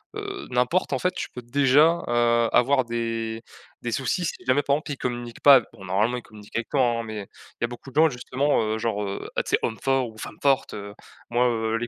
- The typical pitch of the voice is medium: No, low, 120 Hz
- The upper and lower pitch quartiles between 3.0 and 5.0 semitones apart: Yes, average, 3.4 semitones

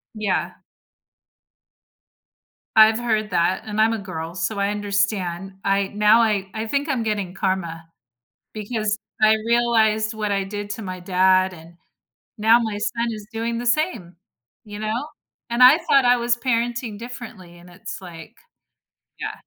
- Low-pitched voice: No, high, 215 Hz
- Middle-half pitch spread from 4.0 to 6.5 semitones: No, average, 3.4 semitones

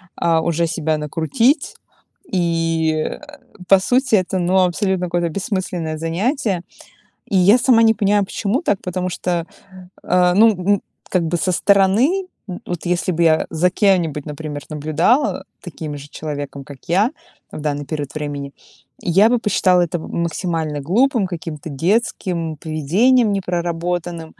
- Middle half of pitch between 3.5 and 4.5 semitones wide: Yes, average, 3.8 semitones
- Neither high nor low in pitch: Yes, medium, 175 Hz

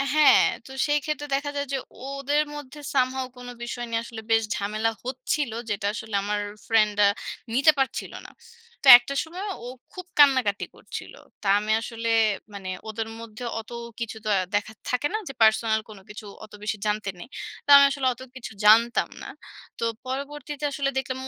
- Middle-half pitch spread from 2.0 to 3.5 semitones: No, average, 4.2 semitones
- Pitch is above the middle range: Yes, high, 245 Hz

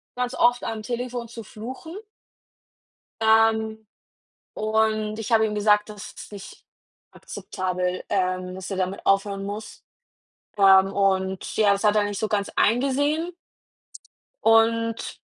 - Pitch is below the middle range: No, high, 215 Hz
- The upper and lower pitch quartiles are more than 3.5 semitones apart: No, narrow, 2.4 semitones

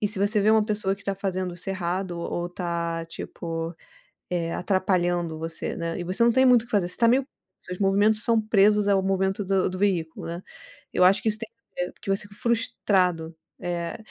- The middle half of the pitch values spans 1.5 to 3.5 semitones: Yes, average, 3.1 semitones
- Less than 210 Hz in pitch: Yes, high, 190 Hz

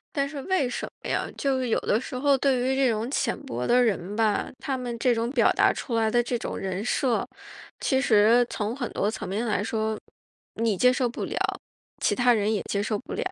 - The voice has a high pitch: Yes, high, 235 Hz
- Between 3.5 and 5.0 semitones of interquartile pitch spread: No, average, 3.1 semitones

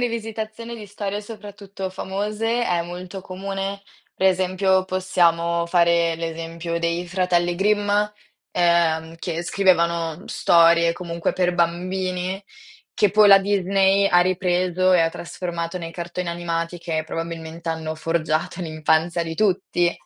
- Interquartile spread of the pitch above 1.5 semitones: Yes, narrow, 2.4 semitones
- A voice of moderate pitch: Yes, medium, 175 Hz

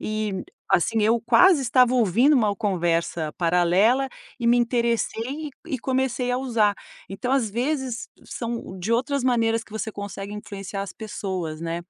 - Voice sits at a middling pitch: No, high, 225 Hz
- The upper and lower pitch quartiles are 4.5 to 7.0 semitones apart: No, average, 4.1 semitones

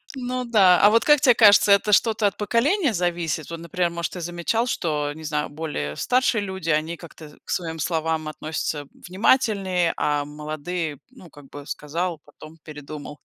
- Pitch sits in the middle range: Yes, medium, 170 Hz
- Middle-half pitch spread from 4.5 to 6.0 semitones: Yes, average, 5.0 semitones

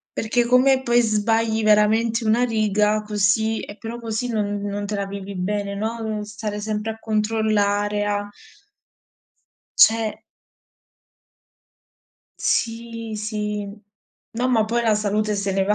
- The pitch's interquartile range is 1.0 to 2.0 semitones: Yes, narrow, 1.5 semitones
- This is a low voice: No, high, 215 Hz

